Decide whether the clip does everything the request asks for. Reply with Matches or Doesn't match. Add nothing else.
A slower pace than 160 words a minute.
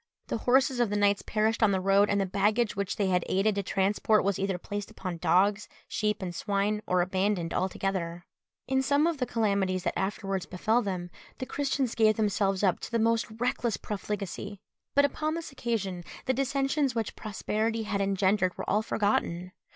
Doesn't match